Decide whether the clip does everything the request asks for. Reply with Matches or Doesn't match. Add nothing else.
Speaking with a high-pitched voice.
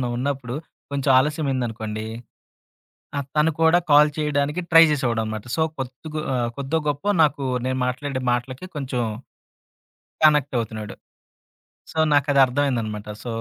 Doesn't match